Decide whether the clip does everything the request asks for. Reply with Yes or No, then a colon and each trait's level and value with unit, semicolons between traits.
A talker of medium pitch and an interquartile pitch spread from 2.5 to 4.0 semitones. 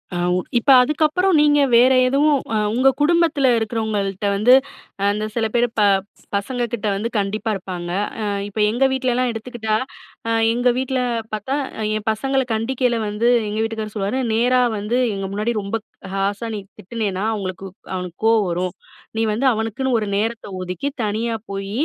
No: high, 225 Hz; average, 3.7 semitones